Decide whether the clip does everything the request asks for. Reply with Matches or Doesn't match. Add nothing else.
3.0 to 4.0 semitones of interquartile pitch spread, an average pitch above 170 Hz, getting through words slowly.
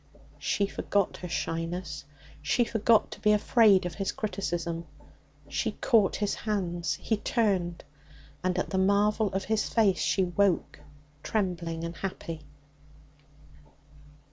Matches